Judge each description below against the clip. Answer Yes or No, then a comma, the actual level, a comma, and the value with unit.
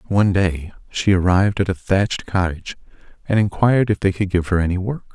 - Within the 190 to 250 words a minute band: Yes, average, 200 wpm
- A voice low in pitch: Yes, very low, 95 Hz